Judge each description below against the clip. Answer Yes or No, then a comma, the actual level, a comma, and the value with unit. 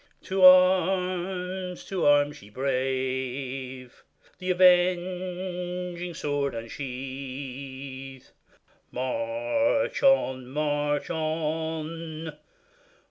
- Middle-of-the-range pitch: Yes, medium, 155 Hz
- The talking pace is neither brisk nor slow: No, slow, 65 wpm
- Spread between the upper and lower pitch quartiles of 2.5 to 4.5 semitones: No, wide, 5.4 semitones